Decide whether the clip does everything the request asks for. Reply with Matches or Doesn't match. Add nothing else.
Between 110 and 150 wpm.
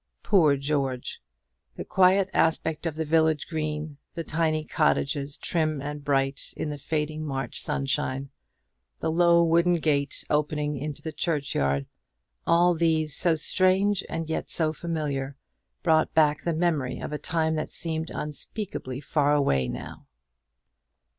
Matches